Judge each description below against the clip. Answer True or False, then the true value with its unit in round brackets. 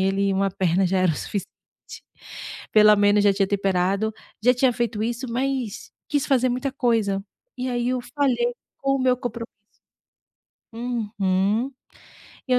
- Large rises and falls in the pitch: False (4.1 semitones)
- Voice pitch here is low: False (225 Hz)